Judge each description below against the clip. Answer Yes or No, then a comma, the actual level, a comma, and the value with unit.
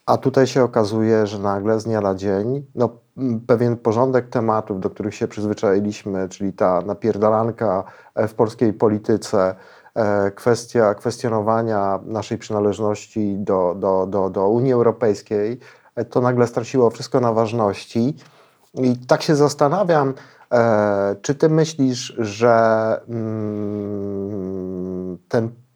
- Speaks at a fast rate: No, average, 115 wpm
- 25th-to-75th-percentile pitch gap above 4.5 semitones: No, average, 3.3 semitones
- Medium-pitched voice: No, low, 110 Hz